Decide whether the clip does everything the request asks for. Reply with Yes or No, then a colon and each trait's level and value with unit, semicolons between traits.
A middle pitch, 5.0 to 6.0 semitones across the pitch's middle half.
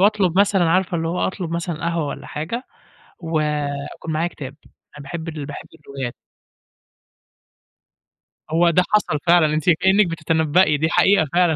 No: medium, 165 Hz; average, 2.7 semitones